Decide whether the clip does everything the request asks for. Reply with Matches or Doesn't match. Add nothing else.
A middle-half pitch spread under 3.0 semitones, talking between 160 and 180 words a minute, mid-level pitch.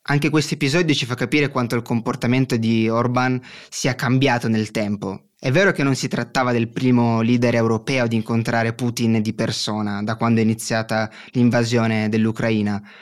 Doesn't match